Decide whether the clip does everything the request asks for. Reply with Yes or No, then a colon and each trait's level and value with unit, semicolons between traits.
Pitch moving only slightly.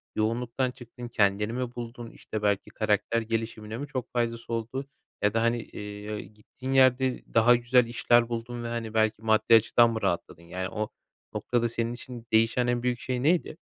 Yes: narrow, 1.9 semitones